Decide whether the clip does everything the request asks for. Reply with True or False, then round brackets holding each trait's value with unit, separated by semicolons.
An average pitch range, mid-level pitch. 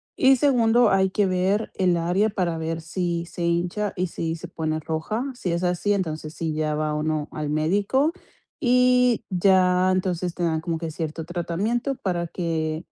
True (3.9 semitones; 175 Hz)